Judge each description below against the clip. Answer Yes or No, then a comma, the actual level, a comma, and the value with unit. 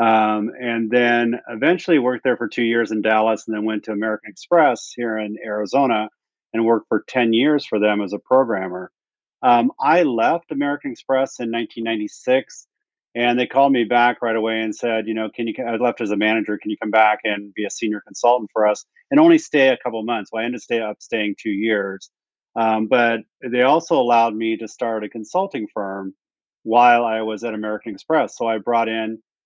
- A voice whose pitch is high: No, low, 115 Hz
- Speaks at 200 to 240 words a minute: Yes, fast, 205 wpm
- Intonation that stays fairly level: Yes, narrow, 2.0 semitones